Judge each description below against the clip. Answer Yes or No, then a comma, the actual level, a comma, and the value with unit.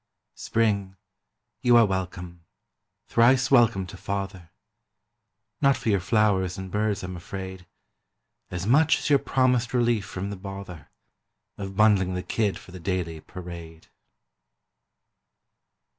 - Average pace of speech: No, slow, 125 wpm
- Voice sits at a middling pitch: No, very low, 95 Hz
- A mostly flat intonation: No, average, 3.8 semitones